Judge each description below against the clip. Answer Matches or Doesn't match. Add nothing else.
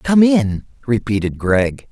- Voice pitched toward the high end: Doesn't match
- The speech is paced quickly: Doesn't match